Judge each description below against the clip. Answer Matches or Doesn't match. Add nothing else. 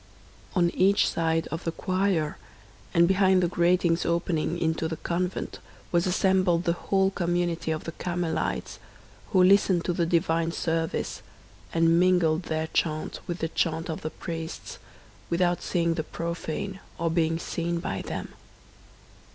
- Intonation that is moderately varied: Doesn't match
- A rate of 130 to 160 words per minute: Matches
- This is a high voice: Doesn't match